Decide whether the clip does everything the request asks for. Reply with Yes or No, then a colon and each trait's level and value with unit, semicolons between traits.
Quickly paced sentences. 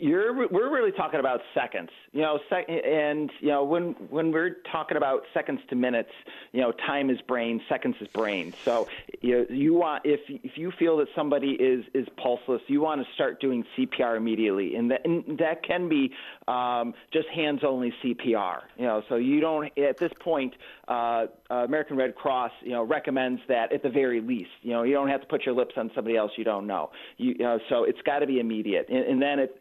Yes: fast, 215 wpm